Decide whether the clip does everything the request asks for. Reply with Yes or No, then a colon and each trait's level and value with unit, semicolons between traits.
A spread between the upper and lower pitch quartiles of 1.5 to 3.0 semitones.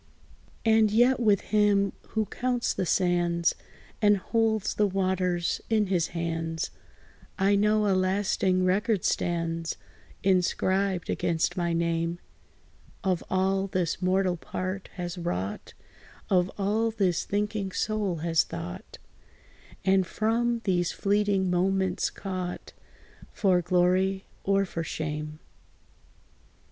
Yes: average, 2.7 semitones